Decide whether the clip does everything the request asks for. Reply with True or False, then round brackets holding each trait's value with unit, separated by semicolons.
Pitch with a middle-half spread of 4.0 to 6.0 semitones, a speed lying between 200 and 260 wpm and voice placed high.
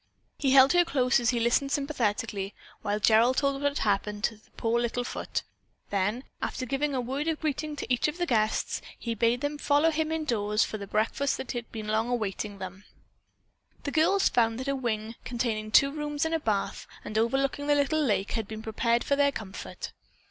True (4.7 semitones; 205 wpm; 245 Hz)